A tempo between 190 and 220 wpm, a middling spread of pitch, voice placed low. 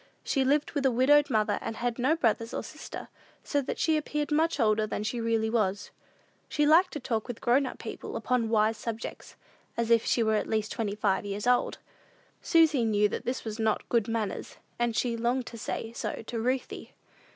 No: average, 200 wpm; average, 3.2 semitones; high, 230 Hz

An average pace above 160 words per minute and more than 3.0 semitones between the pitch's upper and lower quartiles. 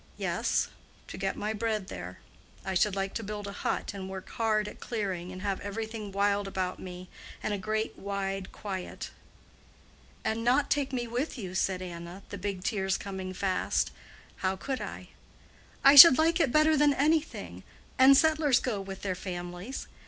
Yes: average, 175 wpm; average, 4.3 semitones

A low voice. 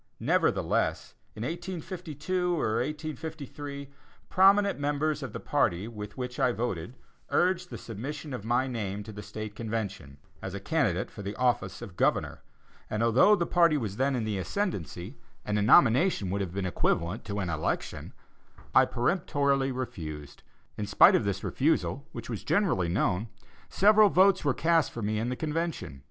Yes: low, 125 Hz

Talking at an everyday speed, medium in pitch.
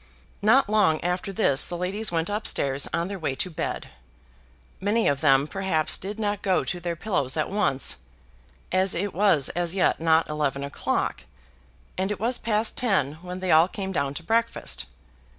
Yes: average, 180 wpm; medium, 180 Hz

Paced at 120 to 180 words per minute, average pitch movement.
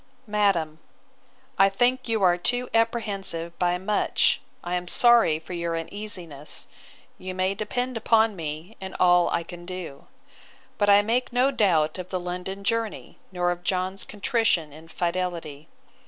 Yes: average, 150 wpm; average, 3.9 semitones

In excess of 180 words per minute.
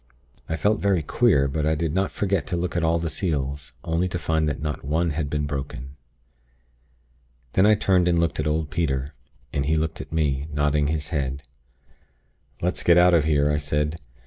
Yes: average, 200 wpm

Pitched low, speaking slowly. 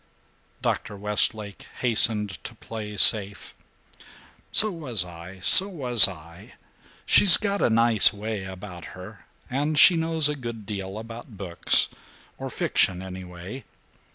Yes: low, 105 Hz; slow, 125 wpm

